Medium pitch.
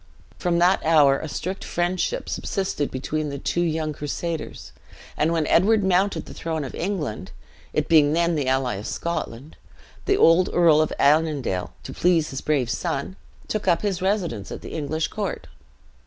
Yes: medium, 160 Hz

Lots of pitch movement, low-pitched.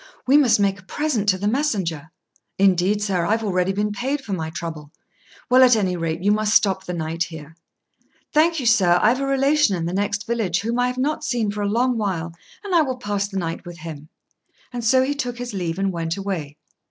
No: wide, 5.9 semitones; high, 205 Hz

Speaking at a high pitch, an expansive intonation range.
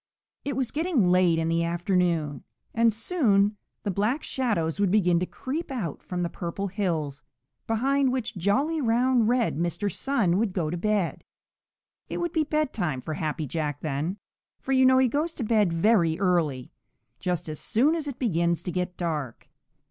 Yes: high, 200 Hz; wide, 7.0 semitones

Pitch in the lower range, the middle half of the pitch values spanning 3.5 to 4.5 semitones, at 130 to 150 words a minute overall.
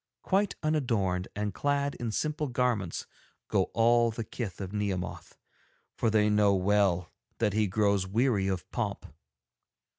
Yes: low, 105 Hz; average, 3.8 semitones; average, 140 wpm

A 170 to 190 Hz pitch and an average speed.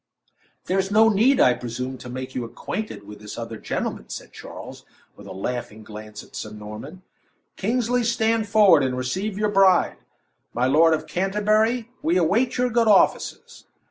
Yes: medium, 185 Hz; average, 165 wpm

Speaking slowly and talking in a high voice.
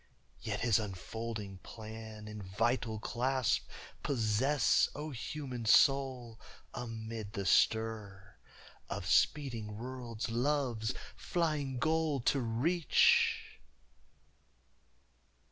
No: slow, 85 wpm; low, 115 Hz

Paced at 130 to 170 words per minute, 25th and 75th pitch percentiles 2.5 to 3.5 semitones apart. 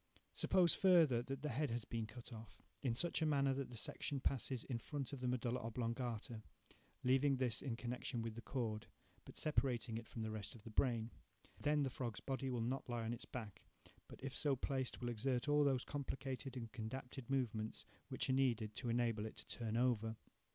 No: fast, 205 wpm; average, 2.8 semitones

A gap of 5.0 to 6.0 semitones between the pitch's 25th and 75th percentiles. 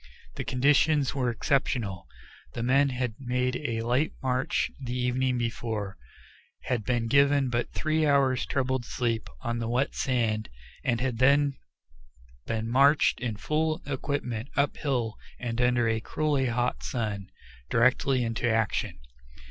No: average, 3.0 semitones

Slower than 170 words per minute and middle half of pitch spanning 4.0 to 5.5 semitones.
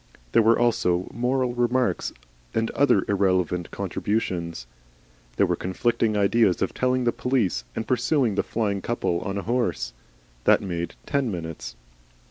Yes: average, 140 wpm; average, 5.1 semitones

